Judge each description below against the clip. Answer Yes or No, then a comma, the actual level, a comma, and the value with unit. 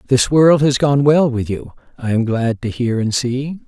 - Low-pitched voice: Yes, low, 130 Hz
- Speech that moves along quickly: Yes, fast, 230 wpm